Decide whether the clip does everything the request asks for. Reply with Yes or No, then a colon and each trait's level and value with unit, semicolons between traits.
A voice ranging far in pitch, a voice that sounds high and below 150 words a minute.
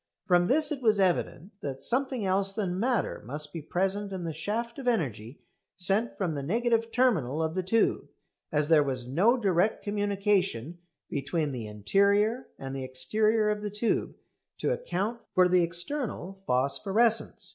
No: wide, 6.4 semitones; high, 195 Hz; average, 160 wpm